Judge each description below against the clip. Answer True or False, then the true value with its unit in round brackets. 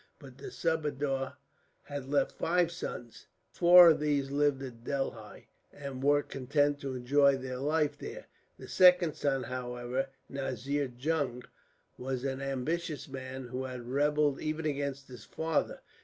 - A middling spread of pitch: False (2.3 semitones)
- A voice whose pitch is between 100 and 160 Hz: True (140 Hz)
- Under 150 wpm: True (140 wpm)